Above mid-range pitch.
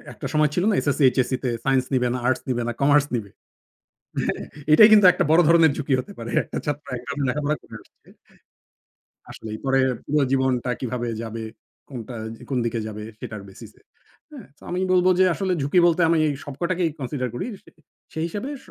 No: medium, 140 Hz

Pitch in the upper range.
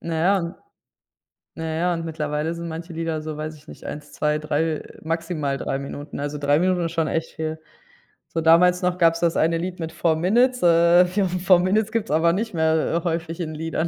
No: medium, 165 Hz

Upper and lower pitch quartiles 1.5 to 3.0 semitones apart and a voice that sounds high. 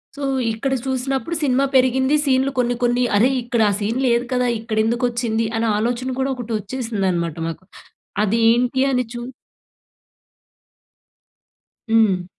Yes: narrow, 2.6 semitones; high, 240 Hz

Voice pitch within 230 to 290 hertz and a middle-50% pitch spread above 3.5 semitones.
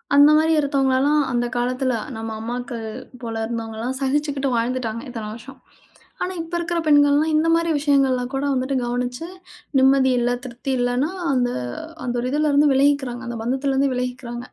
No: very high, 260 Hz; average, 2.8 semitones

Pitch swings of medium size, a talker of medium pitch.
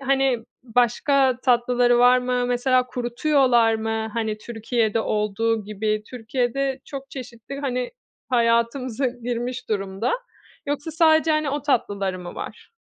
No: average, 3.0 semitones; high, 245 Hz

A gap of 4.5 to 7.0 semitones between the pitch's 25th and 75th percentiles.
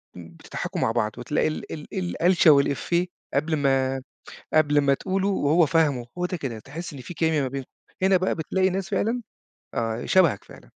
Yes: average, 4.9 semitones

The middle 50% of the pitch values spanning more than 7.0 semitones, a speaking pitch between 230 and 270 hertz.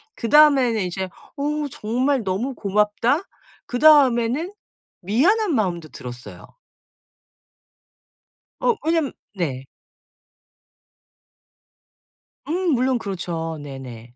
Yes: wide, 8.3 semitones; high, 235 Hz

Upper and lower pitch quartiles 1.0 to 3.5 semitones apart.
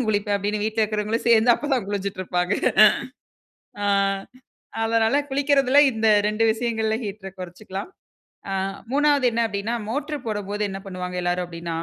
Yes: average, 3.2 semitones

